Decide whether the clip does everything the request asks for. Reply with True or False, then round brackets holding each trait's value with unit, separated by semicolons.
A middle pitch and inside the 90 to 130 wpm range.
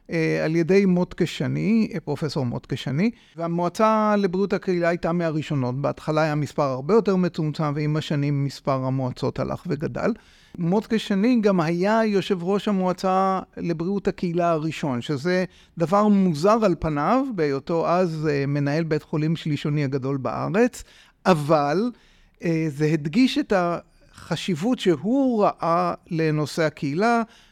True (170 Hz; 115 wpm)